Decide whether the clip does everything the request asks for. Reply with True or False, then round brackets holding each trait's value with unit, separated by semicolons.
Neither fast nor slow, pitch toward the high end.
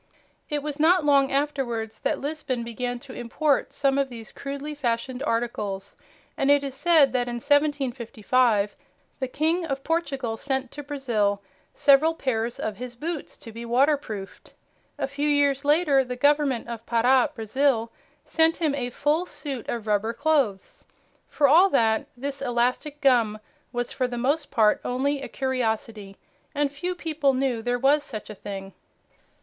True (160 wpm; 265 Hz)